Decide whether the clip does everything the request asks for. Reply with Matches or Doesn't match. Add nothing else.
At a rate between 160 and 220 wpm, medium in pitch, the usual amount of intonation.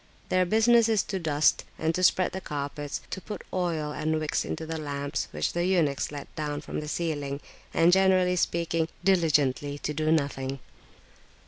Matches